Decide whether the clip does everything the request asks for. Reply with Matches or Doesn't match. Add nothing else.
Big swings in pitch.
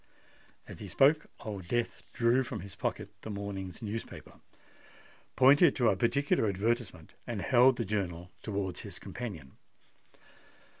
Doesn't match